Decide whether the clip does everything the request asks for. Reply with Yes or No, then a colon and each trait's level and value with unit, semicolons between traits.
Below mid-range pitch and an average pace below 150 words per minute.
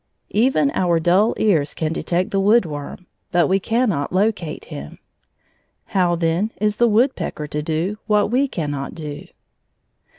No: medium, 180 Hz; average, 140 wpm